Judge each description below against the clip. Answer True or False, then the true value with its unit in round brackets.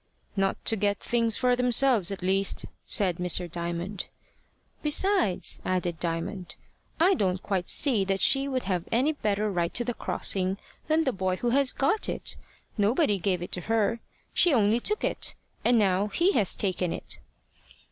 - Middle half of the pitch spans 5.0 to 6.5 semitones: True (5.3 semitones)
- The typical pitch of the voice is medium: False (205 Hz)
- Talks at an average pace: True (165 wpm)